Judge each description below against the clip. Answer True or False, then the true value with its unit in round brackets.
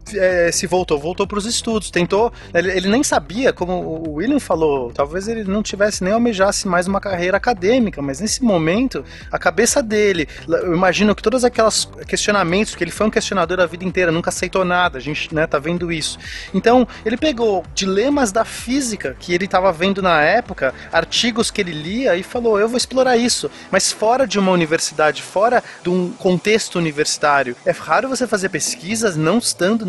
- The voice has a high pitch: True (195 Hz)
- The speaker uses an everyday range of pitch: True (4.3 semitones)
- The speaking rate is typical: False (190 wpm)